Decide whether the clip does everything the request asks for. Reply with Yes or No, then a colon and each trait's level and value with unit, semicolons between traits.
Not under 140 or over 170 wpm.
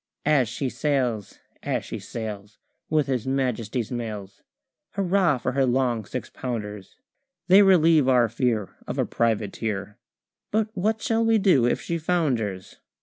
Yes: average, 145 wpm